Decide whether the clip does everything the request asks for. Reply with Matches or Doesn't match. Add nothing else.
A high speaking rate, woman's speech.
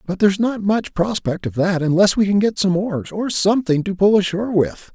Doesn't match